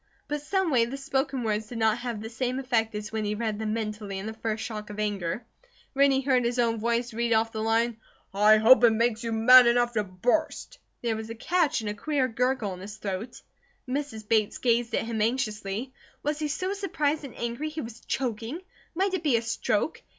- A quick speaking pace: Yes, fast, 215 wpm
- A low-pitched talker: No, high, 230 Hz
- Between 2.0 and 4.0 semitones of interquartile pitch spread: Yes, average, 3.1 semitones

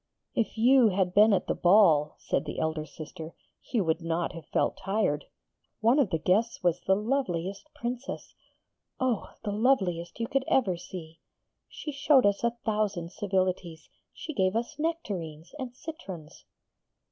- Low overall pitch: No, high, 195 Hz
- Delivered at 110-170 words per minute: Yes, average, 155 wpm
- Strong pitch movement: Yes, wide, 5.7 semitones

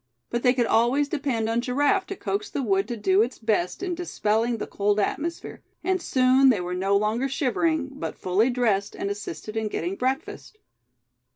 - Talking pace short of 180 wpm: No, average, 185 wpm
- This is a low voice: No, high, 240 Hz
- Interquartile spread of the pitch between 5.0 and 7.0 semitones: Yes, wide, 5.4 semitones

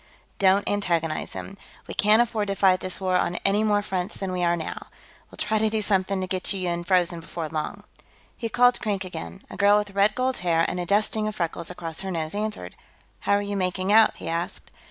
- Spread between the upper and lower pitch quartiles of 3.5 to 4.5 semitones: No, average, 2.9 semitones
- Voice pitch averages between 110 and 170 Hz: No, high, 190 Hz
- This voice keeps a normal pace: No, fast, 220 wpm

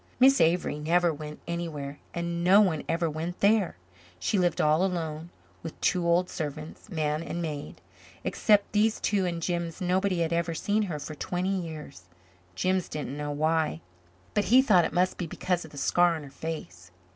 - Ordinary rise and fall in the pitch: Yes, average, 3.0 semitones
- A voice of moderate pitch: Yes, medium, 170 Hz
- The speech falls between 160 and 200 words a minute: Yes, average, 180 wpm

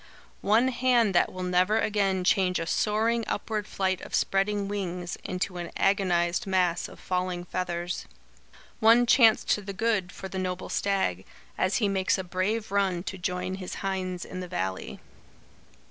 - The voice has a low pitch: No, high, 190 Hz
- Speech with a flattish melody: Yes, narrow, 2.2 semitones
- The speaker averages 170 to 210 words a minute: No, average, 160 wpm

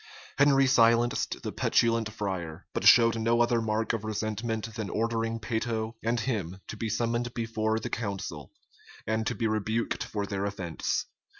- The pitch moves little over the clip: Yes, narrow, 1.4 semitones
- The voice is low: Yes, low, 110 Hz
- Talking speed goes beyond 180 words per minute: No, average, 160 wpm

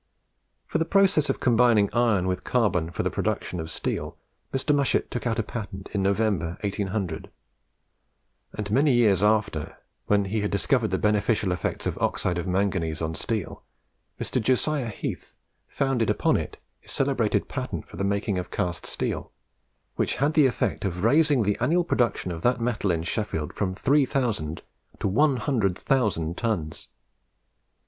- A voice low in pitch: Yes, low, 105 Hz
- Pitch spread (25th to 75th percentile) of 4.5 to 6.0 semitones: Yes, average, 4.9 semitones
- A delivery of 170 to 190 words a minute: No, average, 155 wpm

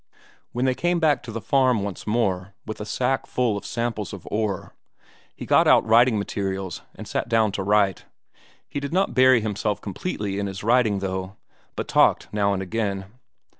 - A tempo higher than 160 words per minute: Yes, average, 185 wpm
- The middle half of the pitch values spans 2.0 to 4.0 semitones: Yes, average, 3.7 semitones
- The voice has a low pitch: Yes, low, 105 Hz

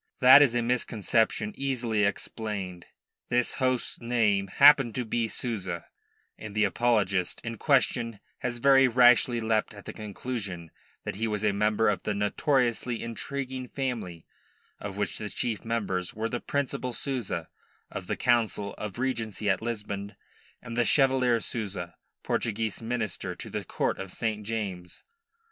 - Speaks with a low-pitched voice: Yes, low, 115 Hz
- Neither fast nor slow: Yes, average, 150 wpm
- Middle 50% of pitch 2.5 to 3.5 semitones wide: Yes, average, 3.2 semitones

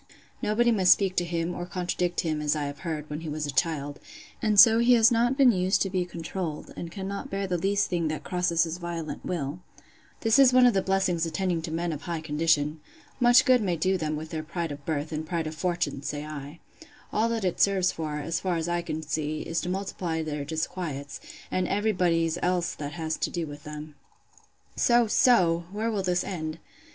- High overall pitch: No, medium, 170 Hz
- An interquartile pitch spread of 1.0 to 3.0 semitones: No, average, 3.5 semitones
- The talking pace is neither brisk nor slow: No, fast, 215 wpm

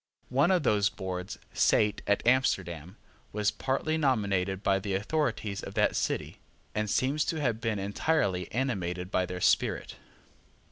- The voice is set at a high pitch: No, low, 105 Hz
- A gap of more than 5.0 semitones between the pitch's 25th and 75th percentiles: Yes, wide, 5.5 semitones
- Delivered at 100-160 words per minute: Yes, average, 145 wpm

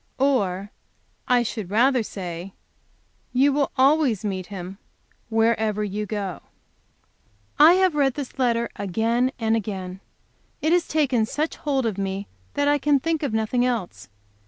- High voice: Yes, high, 230 Hz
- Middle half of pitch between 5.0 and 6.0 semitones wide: Yes, wide, 5.5 semitones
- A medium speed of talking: Yes, average, 145 wpm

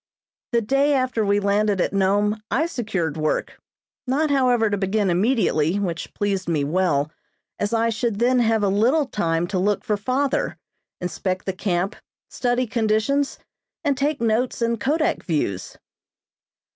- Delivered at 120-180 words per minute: Yes, average, 150 wpm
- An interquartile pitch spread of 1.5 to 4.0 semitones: No, average, 4.8 semitones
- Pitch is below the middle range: No, high, 210 Hz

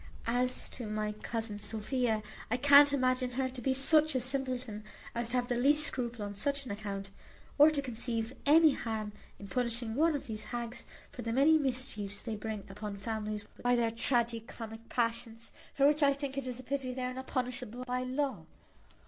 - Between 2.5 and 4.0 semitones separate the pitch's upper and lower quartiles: Yes, average, 3.1 semitones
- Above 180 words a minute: Yes, average, 195 wpm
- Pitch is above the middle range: Yes, high, 245 Hz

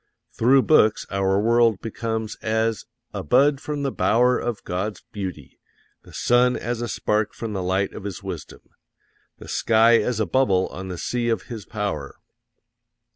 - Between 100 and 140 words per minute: No, average, 165 wpm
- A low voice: Yes, low, 110 Hz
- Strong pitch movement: No, average, 3.4 semitones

